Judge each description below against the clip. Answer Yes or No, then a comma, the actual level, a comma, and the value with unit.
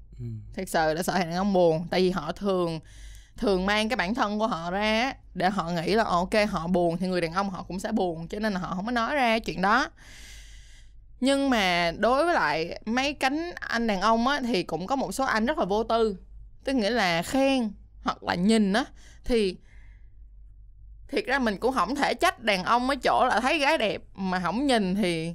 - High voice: Yes, high, 205 Hz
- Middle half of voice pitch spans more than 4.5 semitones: Yes, average, 5.0 semitones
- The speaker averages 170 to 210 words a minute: No, average, 220 wpm